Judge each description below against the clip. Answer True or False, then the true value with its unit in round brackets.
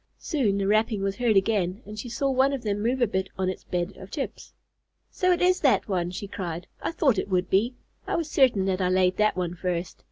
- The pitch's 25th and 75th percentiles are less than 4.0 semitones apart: False (4.9 semitones)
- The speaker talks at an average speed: False (245 wpm)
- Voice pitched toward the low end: False (200 Hz)